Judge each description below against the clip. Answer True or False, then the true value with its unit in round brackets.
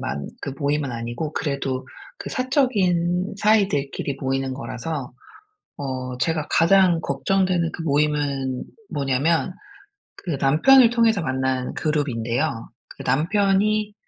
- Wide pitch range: True (6.0 semitones)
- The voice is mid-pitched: True (150 Hz)